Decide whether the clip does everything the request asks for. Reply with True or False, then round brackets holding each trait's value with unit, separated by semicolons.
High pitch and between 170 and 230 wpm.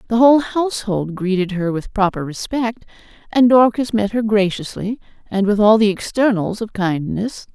False (210 Hz; 160 wpm)